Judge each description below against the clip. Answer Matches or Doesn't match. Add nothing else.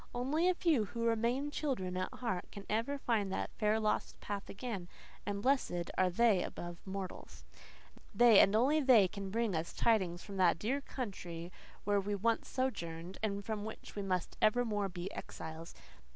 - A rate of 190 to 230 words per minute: Doesn't match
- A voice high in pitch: Matches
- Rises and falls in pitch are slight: Doesn't match